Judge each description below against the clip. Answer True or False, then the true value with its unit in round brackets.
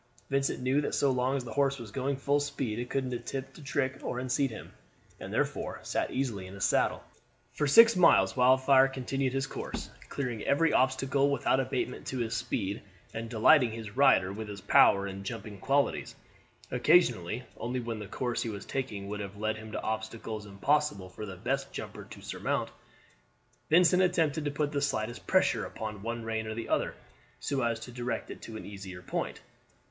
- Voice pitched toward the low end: True (125 Hz)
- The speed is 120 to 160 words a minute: False (195 wpm)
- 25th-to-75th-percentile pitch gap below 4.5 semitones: True (4.0 semitones)